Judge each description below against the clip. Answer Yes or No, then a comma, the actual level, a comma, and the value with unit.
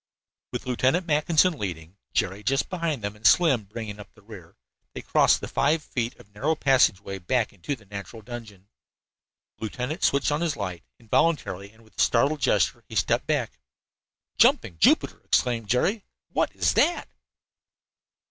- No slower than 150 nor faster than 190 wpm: Yes, average, 155 wpm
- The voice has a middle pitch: No, low, 115 Hz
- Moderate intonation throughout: No, wide, 6.3 semitones